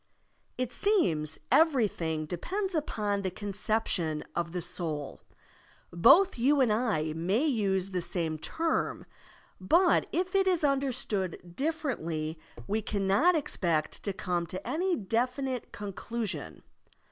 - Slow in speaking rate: Yes, slow, 125 wpm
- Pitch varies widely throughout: Yes, wide, 8.5 semitones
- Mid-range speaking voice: No, high, 205 Hz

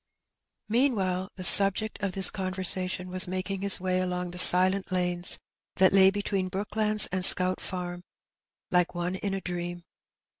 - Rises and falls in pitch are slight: Yes, narrow, 1.5 semitones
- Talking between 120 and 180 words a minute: Yes, average, 155 wpm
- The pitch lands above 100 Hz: Yes, medium, 185 Hz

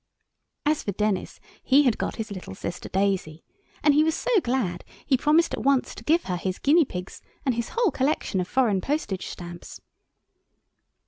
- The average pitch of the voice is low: No, high, 235 Hz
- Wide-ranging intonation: Yes, wide, 7.9 semitones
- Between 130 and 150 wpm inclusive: No, average, 180 wpm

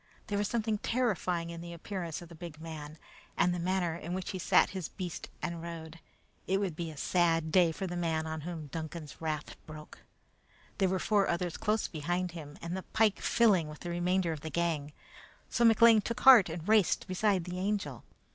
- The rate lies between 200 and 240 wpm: Yes, fast, 205 wpm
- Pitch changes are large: No, average, 2.9 semitones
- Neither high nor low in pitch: Yes, medium, 175 Hz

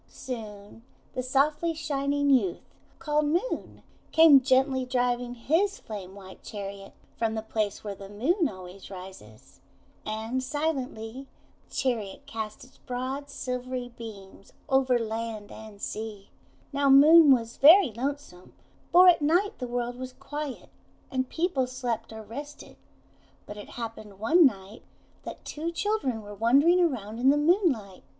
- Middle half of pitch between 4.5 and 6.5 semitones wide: Yes, average, 4.9 semitones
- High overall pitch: Yes, very high, 250 Hz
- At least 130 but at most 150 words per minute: Yes, average, 140 wpm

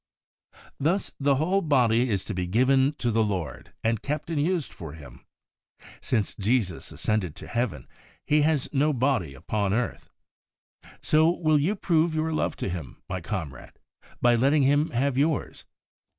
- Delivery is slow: No, average, 160 wpm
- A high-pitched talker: No, low, 130 Hz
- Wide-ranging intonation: Yes, wide, 6.7 semitones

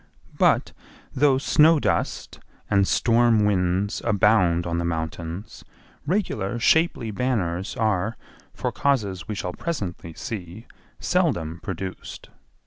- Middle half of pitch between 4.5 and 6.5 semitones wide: Yes, wide, 5.4 semitones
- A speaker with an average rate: No, slow, 110 wpm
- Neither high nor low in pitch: No, low, 100 Hz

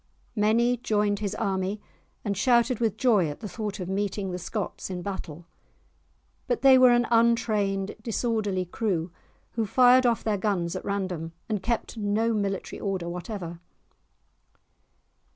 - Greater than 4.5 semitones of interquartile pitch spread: No, average, 3.4 semitones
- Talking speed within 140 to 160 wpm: Yes, average, 145 wpm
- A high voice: Yes, high, 205 Hz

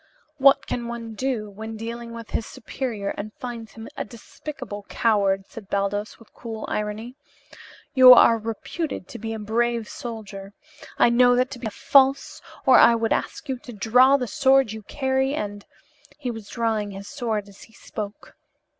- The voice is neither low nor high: No, high, 230 Hz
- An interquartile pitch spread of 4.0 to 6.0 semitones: No, average, 3.1 semitones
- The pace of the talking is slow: No, average, 175 wpm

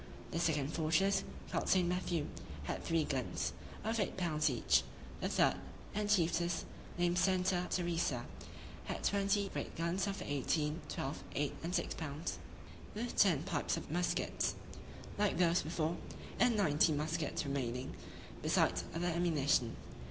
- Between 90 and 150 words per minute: Yes, slow, 135 wpm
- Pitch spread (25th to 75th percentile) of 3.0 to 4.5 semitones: Yes, average, 3.6 semitones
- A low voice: No, medium, 170 Hz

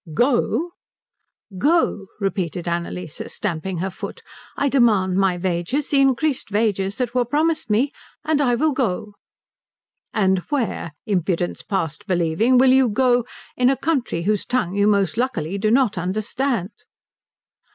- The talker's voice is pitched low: No, high, 215 Hz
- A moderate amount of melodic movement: No, wide, 5.7 semitones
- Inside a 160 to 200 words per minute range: No, slow, 135 wpm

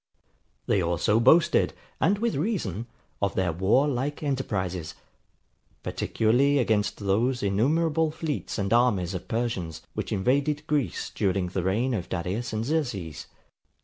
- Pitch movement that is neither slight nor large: No, wide, 7.0 semitones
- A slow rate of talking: Yes, slow, 130 wpm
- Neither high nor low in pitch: No, low, 115 Hz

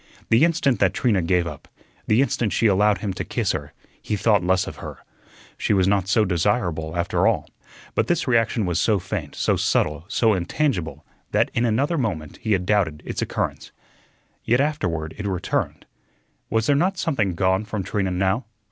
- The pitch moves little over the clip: No, average, 4.5 semitones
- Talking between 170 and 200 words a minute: Yes, average, 185 wpm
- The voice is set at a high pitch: No, low, 100 Hz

